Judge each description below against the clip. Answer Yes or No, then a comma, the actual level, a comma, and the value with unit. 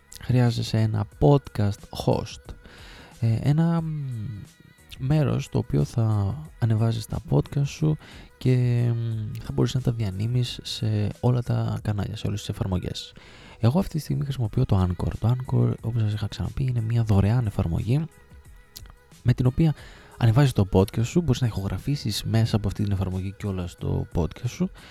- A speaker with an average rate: Yes, average, 155 wpm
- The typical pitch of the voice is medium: No, low, 115 Hz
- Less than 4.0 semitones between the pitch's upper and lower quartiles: No, average, 4.3 semitones